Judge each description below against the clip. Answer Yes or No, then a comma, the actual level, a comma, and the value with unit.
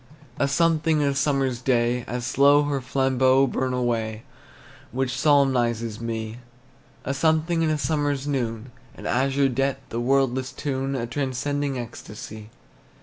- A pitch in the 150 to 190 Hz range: No, low, 135 Hz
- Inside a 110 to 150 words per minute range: Yes, slow, 135 wpm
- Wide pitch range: No, average, 2.7 semitones